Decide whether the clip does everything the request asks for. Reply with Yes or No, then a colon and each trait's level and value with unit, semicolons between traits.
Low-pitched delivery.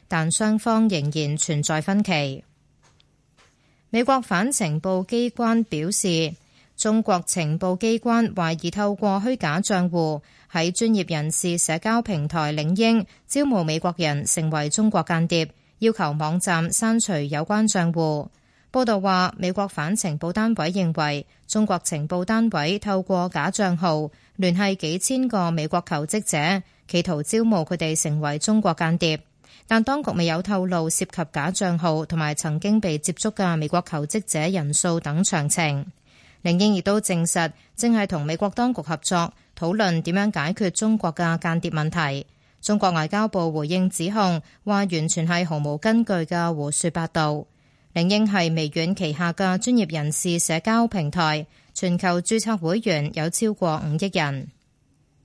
No: medium, 175 Hz